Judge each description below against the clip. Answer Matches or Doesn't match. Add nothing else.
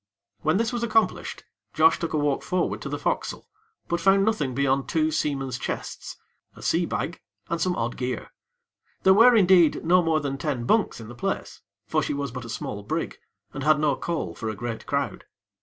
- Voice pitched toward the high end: Doesn't match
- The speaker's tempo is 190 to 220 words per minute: Matches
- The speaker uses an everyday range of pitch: Doesn't match